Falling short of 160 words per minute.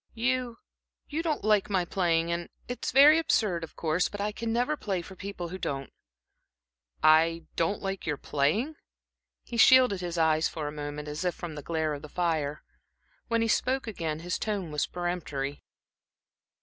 No: average, 175 wpm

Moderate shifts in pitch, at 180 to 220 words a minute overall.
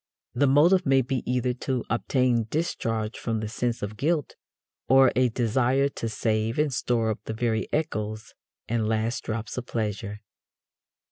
No: average, 3.2 semitones; average, 155 wpm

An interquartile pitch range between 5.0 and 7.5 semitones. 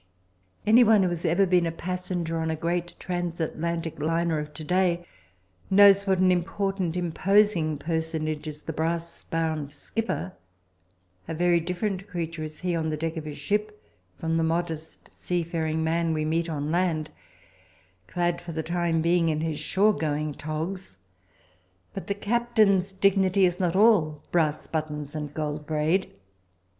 No: average, 2.7 semitones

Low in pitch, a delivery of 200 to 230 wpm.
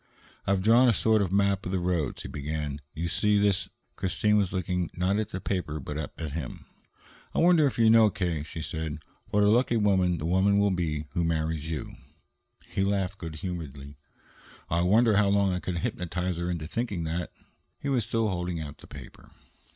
Yes: very low, 90 Hz; fast, 205 wpm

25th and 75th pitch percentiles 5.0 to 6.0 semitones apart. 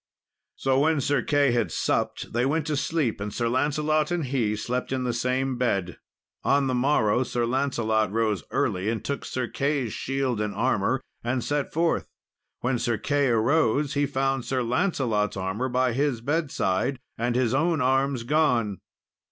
No: average, 3.5 semitones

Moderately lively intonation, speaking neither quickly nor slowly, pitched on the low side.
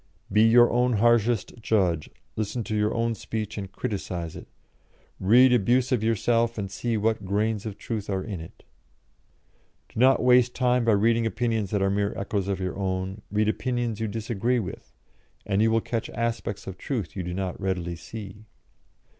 Yes: average, 3.1 semitones; average, 180 wpm; low, 110 Hz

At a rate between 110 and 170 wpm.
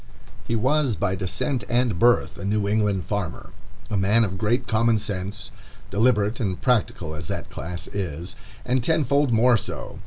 Yes: average, 160 wpm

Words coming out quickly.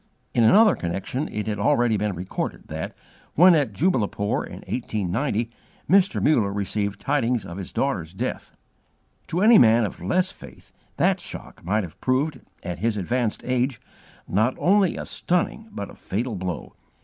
No: average, 160 wpm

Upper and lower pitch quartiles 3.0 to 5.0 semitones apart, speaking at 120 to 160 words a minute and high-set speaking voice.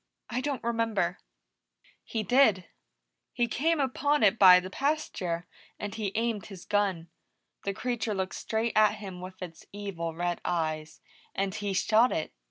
Yes: average, 4.2 semitones; average, 155 wpm; high, 205 Hz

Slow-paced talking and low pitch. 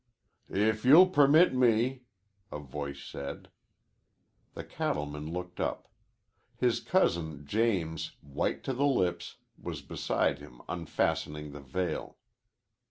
Yes: slow, 110 wpm; very low, 90 Hz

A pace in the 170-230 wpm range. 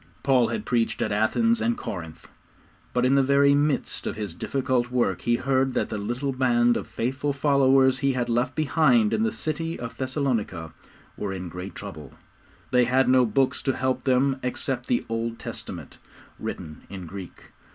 Yes: average, 175 wpm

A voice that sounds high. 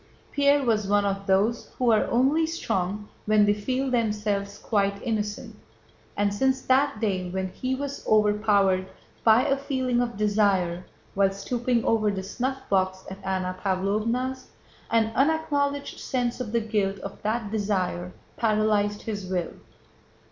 Yes: high, 215 Hz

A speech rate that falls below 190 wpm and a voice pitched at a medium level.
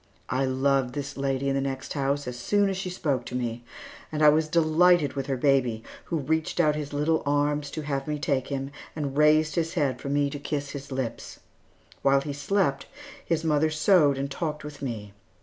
No: fast, 205 wpm; medium, 145 Hz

